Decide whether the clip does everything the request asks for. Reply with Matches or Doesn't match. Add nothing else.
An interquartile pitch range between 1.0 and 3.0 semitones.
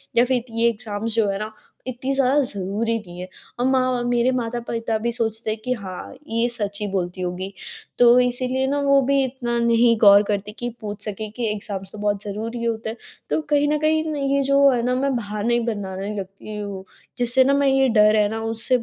Doesn't match